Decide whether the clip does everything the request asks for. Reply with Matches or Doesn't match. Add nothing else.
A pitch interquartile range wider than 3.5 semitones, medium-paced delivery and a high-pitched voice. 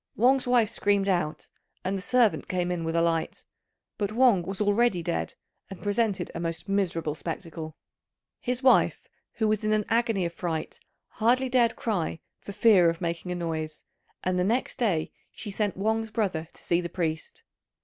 Matches